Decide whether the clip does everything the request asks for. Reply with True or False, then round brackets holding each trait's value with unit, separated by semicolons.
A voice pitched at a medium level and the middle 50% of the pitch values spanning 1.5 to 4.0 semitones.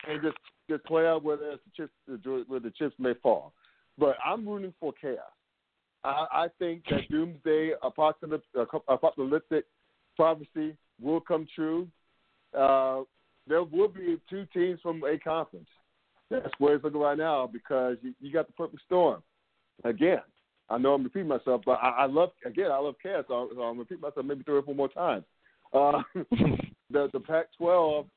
True (155 Hz; 3.3 semitones)